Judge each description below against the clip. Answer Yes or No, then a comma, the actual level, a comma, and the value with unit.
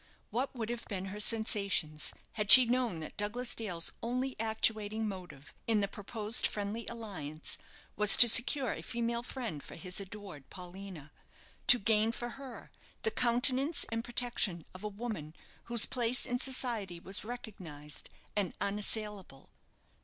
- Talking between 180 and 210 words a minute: No, average, 145 wpm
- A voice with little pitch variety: No, average, 4.0 semitones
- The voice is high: Yes, high, 215 Hz